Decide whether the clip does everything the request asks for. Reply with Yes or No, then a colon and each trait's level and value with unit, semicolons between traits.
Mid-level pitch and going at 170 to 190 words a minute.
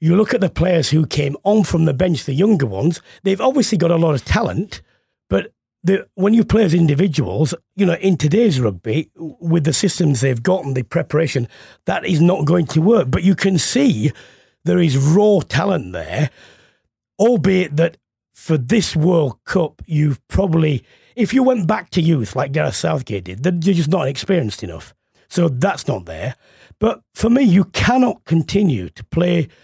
Yes: medium, 170 Hz; average, 185 wpm